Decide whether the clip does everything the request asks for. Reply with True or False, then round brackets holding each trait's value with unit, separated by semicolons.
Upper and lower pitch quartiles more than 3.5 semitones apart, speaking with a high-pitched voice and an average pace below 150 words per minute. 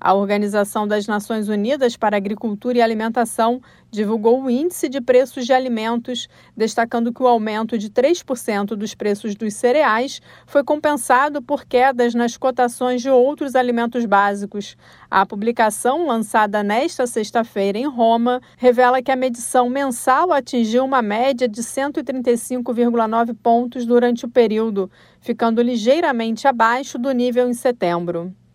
False (2.5 semitones; 240 Hz; 135 wpm)